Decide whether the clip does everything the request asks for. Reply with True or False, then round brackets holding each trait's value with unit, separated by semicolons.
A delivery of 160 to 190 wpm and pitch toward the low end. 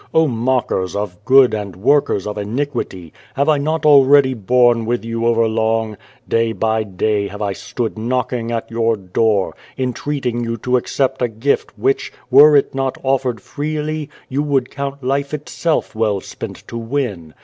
True (165 wpm; 120 Hz)